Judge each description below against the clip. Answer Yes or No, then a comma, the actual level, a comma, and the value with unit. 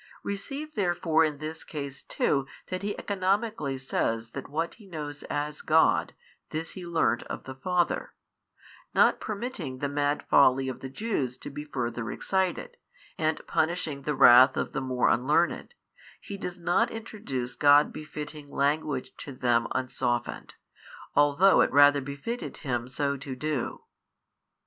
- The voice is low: No, medium, 145 Hz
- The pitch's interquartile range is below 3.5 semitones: No, average, 4.7 semitones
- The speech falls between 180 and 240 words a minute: No, average, 145 wpm